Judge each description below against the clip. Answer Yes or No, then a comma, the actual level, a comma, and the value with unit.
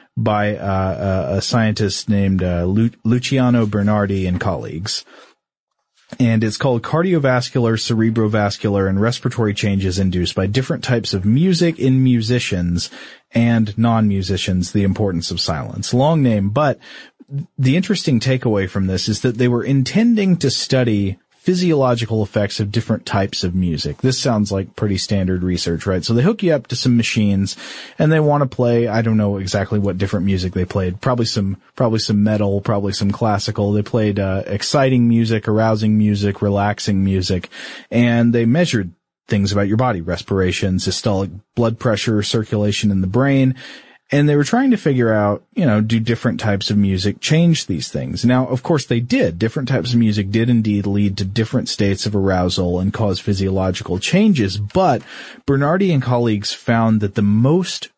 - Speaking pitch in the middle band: No, low, 110 Hz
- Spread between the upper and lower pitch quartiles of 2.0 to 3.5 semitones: No, average, 3.9 semitones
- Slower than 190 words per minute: Yes, average, 170 wpm